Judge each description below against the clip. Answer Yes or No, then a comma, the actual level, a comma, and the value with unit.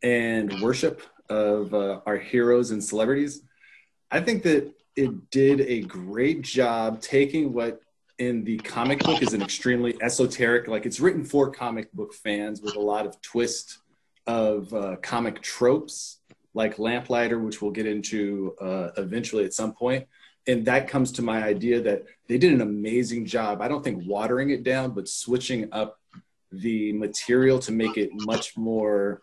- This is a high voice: No, low, 115 Hz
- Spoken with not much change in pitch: No, average, 3.4 semitones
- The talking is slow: No, average, 165 wpm